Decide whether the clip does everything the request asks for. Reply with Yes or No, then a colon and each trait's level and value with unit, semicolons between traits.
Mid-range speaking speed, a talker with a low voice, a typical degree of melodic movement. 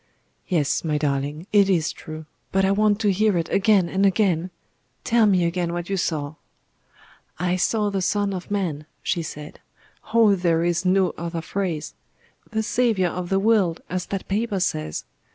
No: average, 170 wpm; medium, 185 Hz; average, 3.3 semitones